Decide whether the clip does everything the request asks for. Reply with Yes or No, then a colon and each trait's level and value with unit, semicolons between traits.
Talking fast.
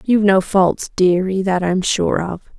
No: average, 185 wpm